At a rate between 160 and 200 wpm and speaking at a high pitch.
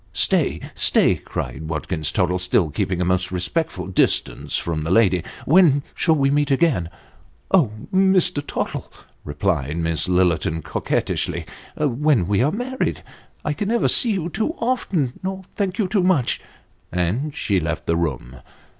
No: average, 170 wpm; low, 115 Hz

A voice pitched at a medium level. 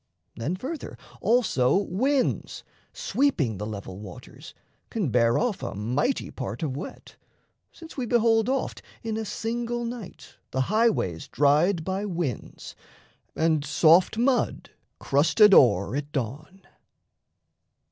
Yes: medium, 180 Hz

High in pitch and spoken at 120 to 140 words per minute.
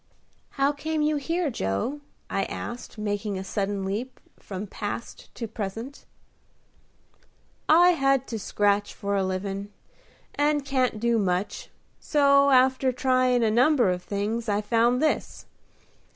Yes: high, 235 Hz; slow, 135 wpm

